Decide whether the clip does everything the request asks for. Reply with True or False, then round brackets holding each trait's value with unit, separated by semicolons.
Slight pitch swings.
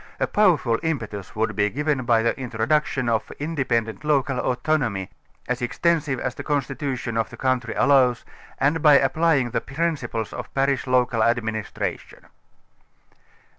False (4.0 semitones)